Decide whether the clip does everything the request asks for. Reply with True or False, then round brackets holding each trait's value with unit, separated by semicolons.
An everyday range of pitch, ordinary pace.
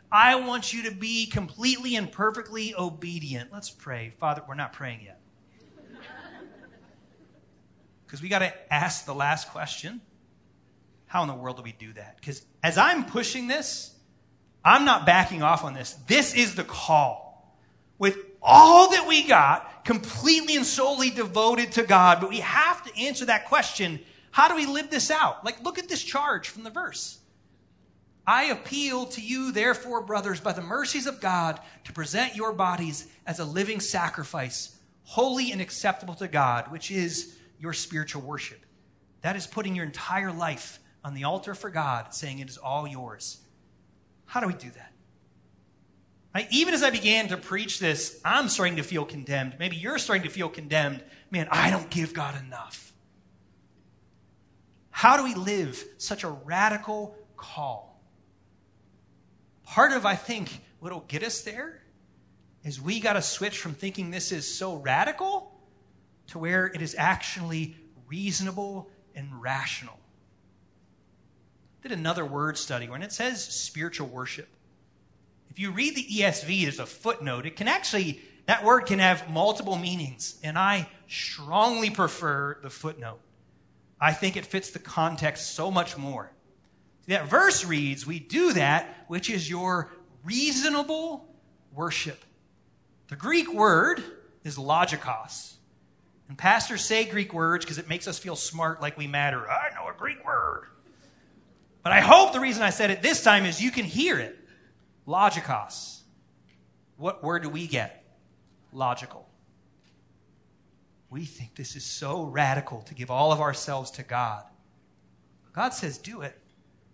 False (7.4 semitones; 155 wpm)